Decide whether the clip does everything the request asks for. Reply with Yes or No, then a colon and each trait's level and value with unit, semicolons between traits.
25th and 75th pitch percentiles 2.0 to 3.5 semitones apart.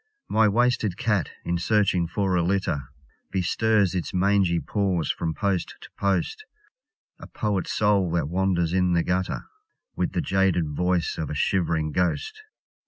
Yes: average, 2.9 semitones